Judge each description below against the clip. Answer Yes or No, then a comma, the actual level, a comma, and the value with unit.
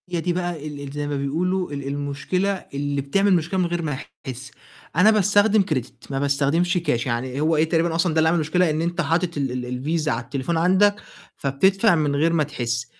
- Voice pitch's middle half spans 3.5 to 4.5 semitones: Yes, average, 4.1 semitones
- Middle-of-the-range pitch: Yes, medium, 155 Hz